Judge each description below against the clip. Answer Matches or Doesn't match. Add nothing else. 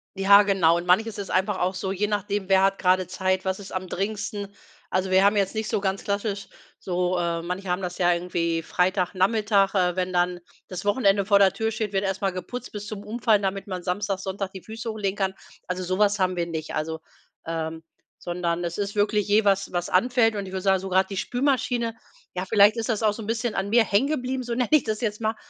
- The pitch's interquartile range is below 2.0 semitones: Doesn't match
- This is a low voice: Doesn't match